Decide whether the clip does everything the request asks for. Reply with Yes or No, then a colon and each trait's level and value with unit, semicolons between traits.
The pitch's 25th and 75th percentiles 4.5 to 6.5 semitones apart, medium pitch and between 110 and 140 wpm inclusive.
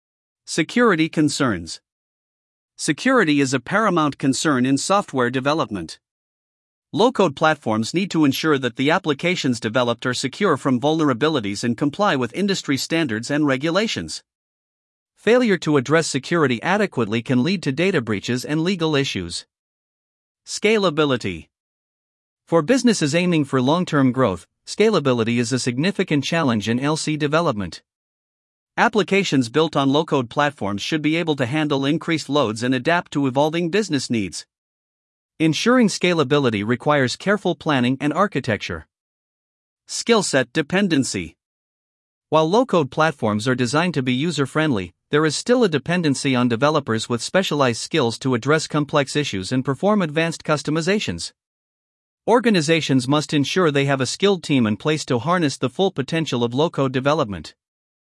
Yes: average, 4.8 semitones; medium, 145 Hz; slow, 135 wpm